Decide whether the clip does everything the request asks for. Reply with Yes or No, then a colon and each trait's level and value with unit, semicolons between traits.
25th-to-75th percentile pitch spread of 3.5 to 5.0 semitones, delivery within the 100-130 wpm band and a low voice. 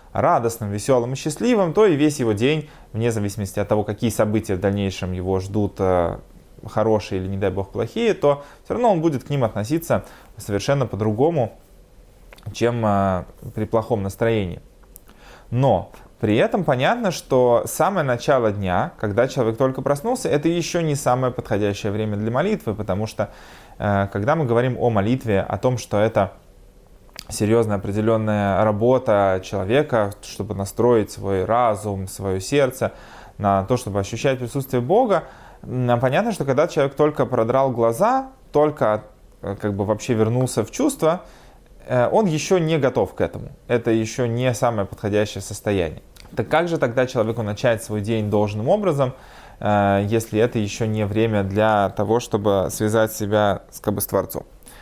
No: average, 4.1 semitones; average, 150 wpm; low, 110 Hz